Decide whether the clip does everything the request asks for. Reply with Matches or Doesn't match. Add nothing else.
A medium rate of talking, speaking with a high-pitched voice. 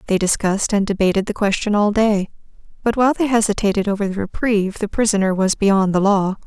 Matches